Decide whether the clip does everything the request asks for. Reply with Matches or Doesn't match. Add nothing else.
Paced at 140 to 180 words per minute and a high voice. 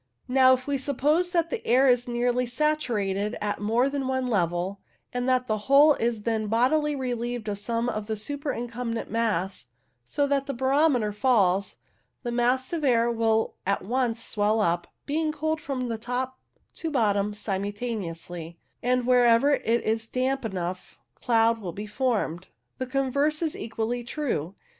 Matches